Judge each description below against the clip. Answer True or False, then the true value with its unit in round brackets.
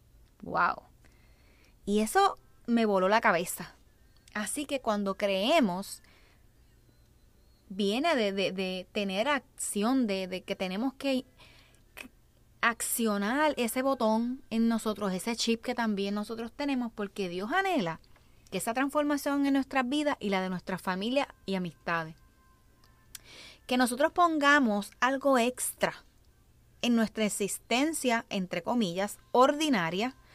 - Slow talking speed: True (120 wpm)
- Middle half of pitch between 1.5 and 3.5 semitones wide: False (5.1 semitones)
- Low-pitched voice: False (230 Hz)